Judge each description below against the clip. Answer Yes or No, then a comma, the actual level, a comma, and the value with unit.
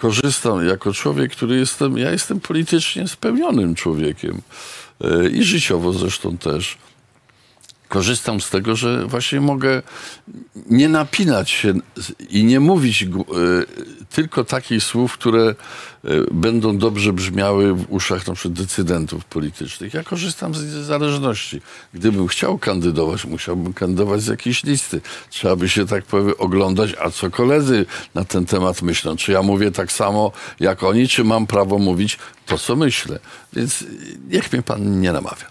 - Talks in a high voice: No, low, 100 Hz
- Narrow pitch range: No, average, 5.2 semitones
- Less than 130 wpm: No, average, 140 wpm